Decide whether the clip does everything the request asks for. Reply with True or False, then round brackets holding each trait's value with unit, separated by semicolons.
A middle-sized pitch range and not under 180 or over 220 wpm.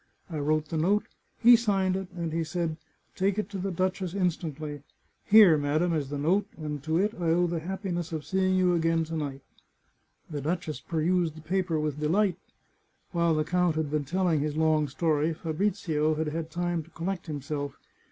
True (3.0 semitones; 190 wpm)